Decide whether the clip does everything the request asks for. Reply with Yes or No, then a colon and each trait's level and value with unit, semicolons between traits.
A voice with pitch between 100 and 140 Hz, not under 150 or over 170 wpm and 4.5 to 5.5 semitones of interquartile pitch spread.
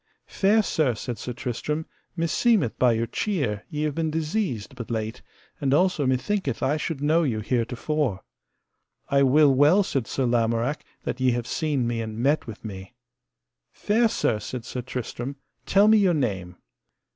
Yes: low, 135 Hz; average, 165 wpm; average, 5.2 semitones